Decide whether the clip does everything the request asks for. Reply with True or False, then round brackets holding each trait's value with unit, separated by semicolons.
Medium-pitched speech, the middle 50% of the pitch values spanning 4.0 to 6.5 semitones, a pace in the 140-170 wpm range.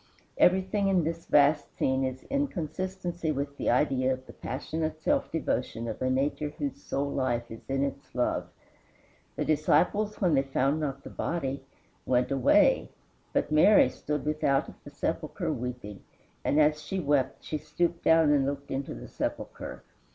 False (145 Hz; 3.4 semitones; 165 wpm)